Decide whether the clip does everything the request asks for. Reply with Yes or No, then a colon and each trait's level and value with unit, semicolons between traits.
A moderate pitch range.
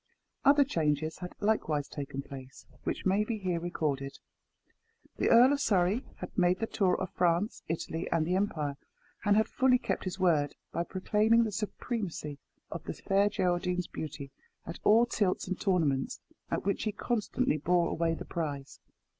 Yes: average, 5.0 semitones